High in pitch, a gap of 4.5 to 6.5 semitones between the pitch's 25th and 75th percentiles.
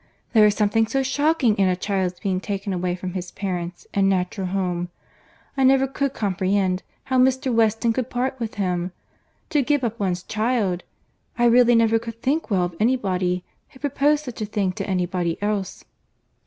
Yes: high, 210 Hz; average, 5.2 semitones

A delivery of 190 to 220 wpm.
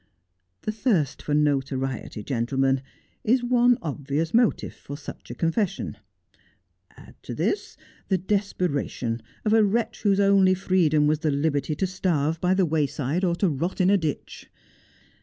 No: average, 155 wpm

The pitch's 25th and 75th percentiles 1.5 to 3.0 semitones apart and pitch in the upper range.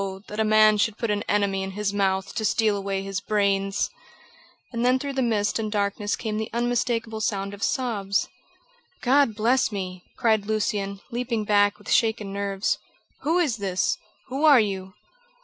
Yes: narrow, 2.6 semitones; high, 210 Hz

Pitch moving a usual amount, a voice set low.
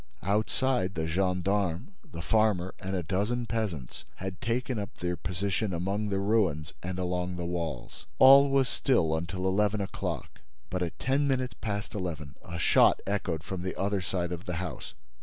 Yes: average, 3.4 semitones; very low, 95 Hz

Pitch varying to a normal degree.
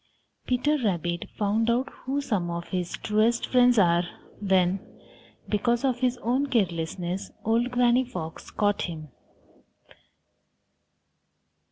No: wide, 5.7 semitones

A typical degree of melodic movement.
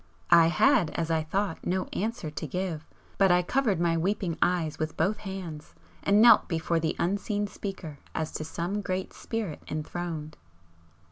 Yes: average, 3.7 semitones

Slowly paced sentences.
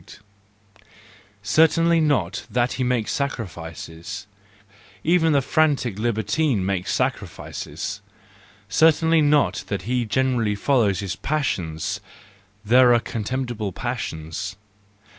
Yes: slow, 95 wpm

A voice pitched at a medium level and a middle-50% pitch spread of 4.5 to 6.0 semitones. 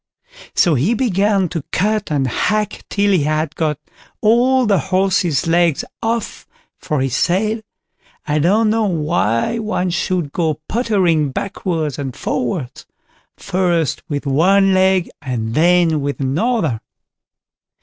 Yes: medium, 175 Hz; average, 5.3 semitones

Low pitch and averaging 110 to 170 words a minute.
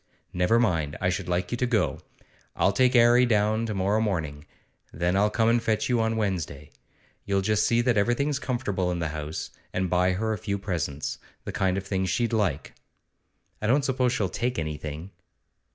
No: low, 100 Hz; average, 190 wpm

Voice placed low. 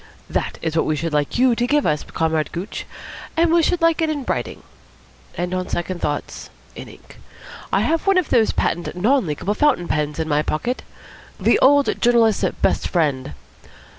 No: medium, 185 Hz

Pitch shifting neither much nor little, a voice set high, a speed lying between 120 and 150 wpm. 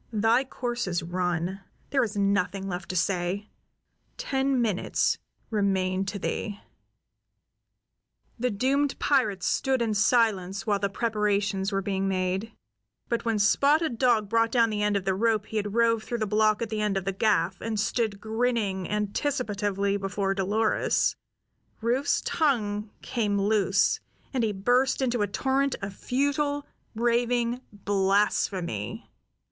Yes: average, 3.3 semitones; high, 210 Hz; average, 140 wpm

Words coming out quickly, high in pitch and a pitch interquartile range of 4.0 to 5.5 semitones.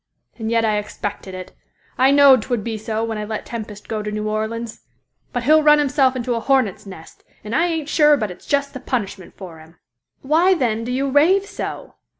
Yes: fast, 210 wpm; high, 230 Hz; average, 4.8 semitones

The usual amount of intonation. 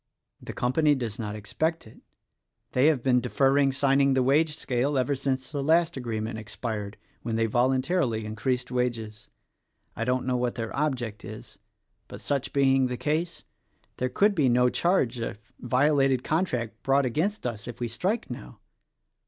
Yes: average, 3.4 semitones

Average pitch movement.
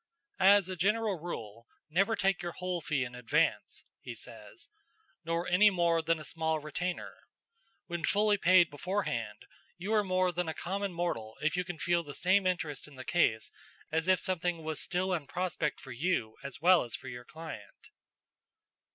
Yes: average, 3.3 semitones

